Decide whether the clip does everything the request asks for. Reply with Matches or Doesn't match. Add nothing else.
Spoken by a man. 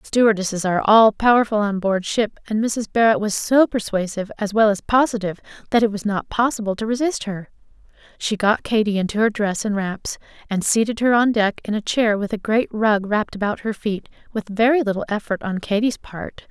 Doesn't match